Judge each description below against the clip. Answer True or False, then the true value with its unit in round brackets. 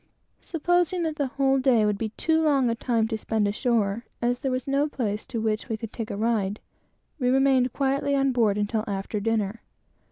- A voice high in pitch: True (240 Hz)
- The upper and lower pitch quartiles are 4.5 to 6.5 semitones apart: False (4.0 semitones)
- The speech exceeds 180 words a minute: True (200 wpm)